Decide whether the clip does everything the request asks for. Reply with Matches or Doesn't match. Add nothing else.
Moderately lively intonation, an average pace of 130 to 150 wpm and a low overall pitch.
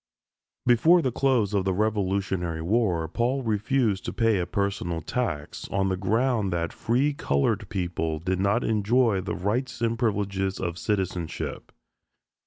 Matches